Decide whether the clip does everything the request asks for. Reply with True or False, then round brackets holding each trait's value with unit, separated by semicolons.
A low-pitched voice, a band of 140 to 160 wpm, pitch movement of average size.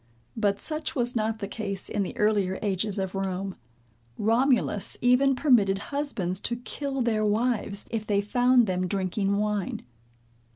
False (210 Hz; 150 wpm; 3.7 semitones)